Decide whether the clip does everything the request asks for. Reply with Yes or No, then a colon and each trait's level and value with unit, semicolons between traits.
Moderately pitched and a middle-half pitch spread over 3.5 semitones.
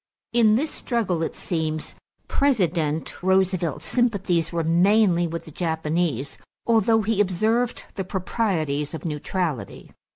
Yes: medium, 180 Hz; average, 5.0 semitones